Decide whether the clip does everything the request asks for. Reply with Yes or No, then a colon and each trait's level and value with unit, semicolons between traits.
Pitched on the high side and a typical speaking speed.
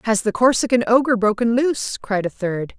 Yes: high, 225 Hz; average, 195 wpm